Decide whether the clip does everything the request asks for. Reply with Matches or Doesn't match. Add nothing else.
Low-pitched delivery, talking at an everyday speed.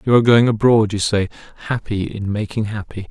Matches